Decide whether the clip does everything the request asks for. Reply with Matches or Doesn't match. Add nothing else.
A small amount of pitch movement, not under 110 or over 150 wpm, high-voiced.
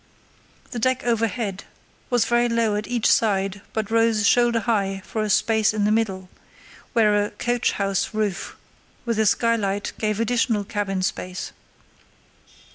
Matches